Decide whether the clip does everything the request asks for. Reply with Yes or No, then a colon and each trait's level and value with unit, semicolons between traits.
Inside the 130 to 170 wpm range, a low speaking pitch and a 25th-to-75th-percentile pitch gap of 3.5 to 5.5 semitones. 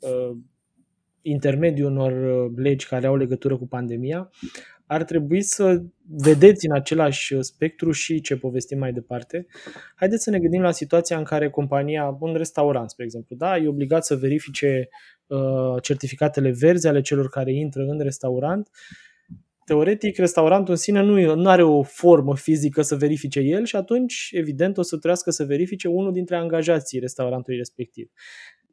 No: average, 150 wpm; medium, 150 Hz; average, 4.2 semitones